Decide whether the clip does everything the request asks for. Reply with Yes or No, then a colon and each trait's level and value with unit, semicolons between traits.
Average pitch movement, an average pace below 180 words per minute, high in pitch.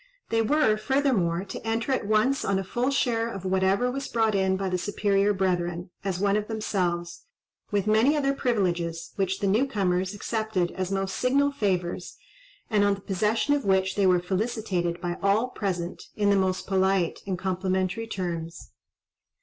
Yes: average, 3.4 semitones; average, 170 wpm; high, 195 Hz